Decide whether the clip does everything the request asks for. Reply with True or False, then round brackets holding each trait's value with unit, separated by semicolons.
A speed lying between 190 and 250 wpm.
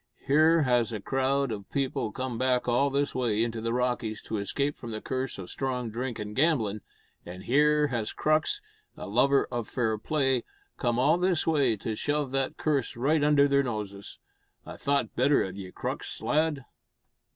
False (180 wpm)